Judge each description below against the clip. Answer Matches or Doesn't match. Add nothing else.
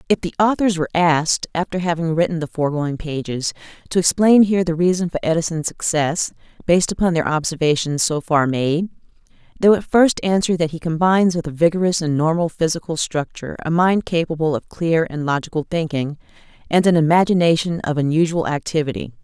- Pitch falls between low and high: Matches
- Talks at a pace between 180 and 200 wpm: Doesn't match